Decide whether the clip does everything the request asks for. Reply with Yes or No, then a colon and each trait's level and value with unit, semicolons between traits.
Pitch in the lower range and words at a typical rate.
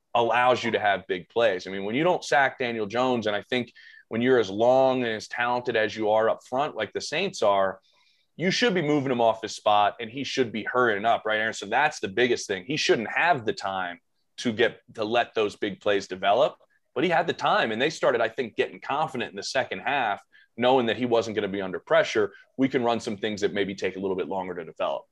No: low, 115 Hz; fast, 255 wpm